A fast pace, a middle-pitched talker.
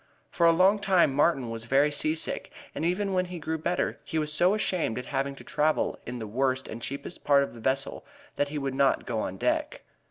Yes: fast, 225 wpm; medium, 145 Hz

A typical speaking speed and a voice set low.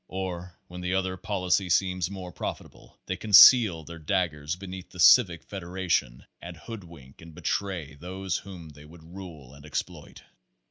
Yes: average, 150 wpm; very low, 90 Hz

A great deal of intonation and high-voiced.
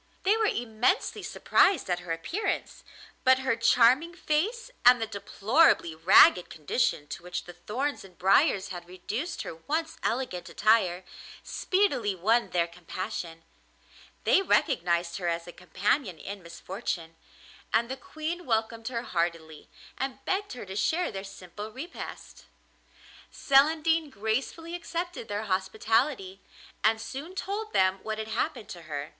Yes: wide, 8.0 semitones; high, 220 Hz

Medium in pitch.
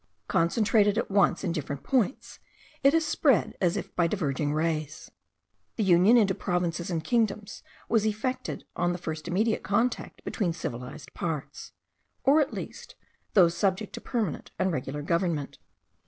Yes: medium, 180 Hz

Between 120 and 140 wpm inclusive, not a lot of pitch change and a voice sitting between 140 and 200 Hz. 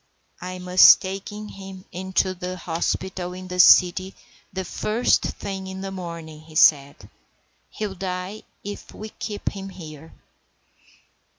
Yes: slow, 135 wpm; narrow, 1.4 semitones; medium, 185 Hz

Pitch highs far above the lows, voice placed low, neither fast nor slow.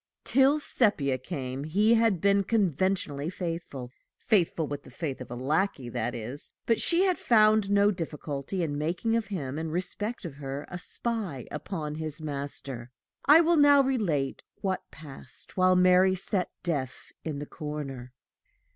No: wide, 6.3 semitones; medium, 165 Hz; average, 155 wpm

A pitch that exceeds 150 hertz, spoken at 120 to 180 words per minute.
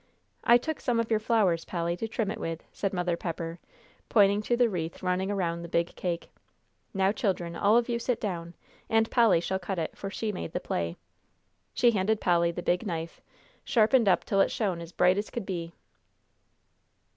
No: high, 190 Hz; average, 195 wpm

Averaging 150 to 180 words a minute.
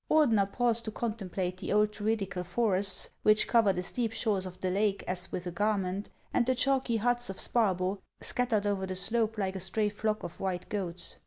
No: average, 200 wpm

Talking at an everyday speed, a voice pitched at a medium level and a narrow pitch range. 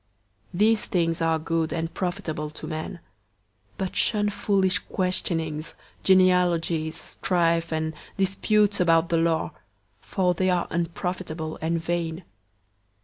No: slow, 120 wpm; medium, 170 Hz; narrow, 2.3 semitones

